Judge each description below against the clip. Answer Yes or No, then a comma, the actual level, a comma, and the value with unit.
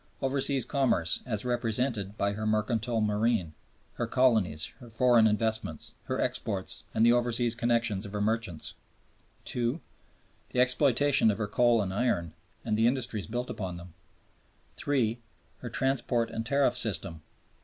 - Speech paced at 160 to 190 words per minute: No, average, 145 wpm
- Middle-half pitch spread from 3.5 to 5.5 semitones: No, average, 2.9 semitones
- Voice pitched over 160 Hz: No, low, 115 Hz